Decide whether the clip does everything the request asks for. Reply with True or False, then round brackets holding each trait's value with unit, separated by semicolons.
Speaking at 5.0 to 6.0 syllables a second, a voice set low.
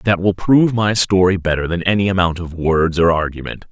True (5.5 syllables/s; 90 Hz)